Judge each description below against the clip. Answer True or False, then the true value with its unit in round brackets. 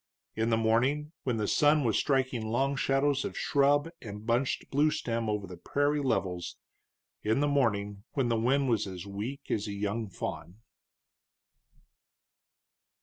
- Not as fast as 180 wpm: True (145 wpm)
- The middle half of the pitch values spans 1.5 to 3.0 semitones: False (4.9 semitones)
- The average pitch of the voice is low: True (115 Hz)